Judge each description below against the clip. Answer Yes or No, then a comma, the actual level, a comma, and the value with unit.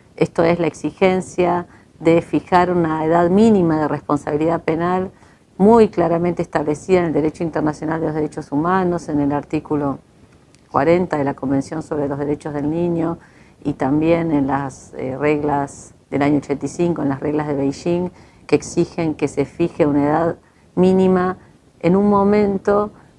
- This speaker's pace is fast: No, average, 155 wpm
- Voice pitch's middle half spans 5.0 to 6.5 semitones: No, average, 3.0 semitones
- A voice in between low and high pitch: Yes, medium, 160 Hz